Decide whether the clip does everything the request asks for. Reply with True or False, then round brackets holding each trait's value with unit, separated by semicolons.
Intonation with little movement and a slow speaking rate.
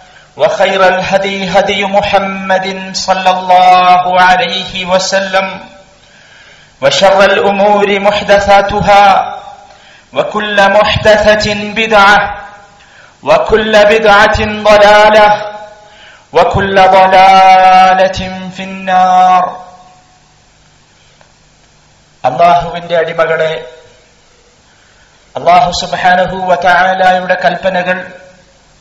True (1.8 semitones; 55 wpm)